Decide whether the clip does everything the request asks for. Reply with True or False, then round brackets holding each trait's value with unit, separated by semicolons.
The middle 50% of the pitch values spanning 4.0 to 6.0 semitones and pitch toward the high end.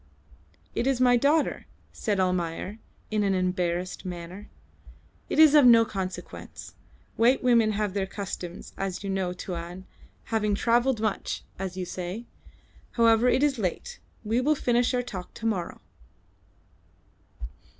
True (4.6 semitones; 210 Hz)